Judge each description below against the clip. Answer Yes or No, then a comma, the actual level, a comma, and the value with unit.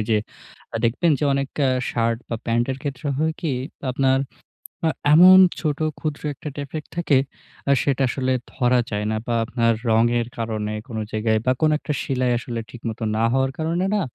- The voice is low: Yes, low, 130 Hz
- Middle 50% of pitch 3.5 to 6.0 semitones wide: Yes, average, 4.0 semitones